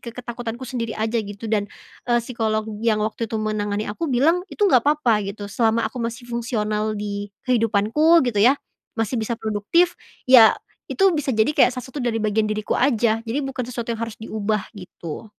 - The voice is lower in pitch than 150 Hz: No, high, 225 Hz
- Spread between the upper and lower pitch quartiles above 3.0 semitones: No, average, 2.7 semitones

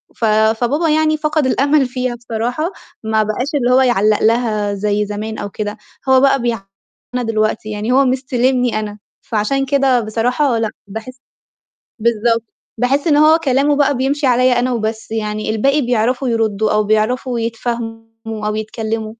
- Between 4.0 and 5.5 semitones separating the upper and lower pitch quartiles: No, average, 3.3 semitones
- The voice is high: Yes, high, 235 Hz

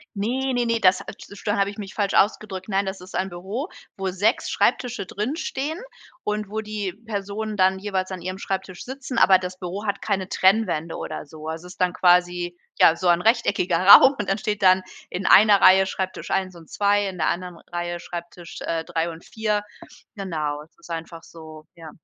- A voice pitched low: No, high, 190 Hz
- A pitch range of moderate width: Yes, average, 3.0 semitones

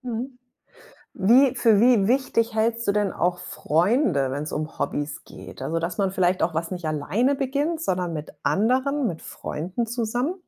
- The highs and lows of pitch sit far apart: Yes, wide, 6.8 semitones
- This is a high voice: Yes, high, 215 Hz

